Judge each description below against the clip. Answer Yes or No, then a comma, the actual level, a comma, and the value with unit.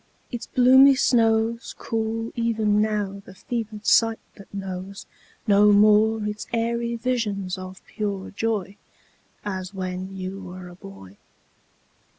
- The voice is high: Yes, high, 210 Hz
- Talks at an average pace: No, slow, 125 wpm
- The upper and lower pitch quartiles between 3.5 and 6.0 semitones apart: No, average, 3.0 semitones